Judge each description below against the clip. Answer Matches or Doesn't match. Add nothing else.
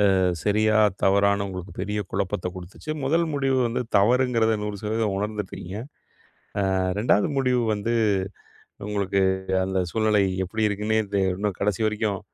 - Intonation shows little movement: Matches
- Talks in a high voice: Doesn't match